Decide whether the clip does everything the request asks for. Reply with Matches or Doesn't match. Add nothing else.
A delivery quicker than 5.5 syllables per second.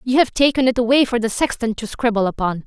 Matches